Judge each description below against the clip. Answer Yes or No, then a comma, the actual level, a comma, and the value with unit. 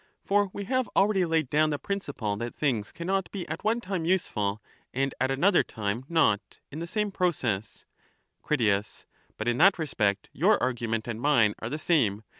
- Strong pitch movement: Yes, wide, 8.6 semitones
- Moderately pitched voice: Yes, medium, 145 Hz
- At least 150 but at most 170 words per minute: No, average, 180 wpm